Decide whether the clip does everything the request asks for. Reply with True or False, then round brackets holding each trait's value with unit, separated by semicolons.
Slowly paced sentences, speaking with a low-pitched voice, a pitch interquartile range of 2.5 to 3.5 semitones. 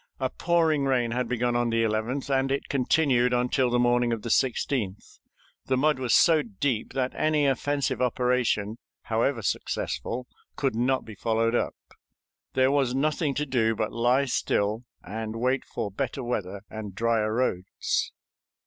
False (155 wpm; 125 Hz; 2.9 semitones)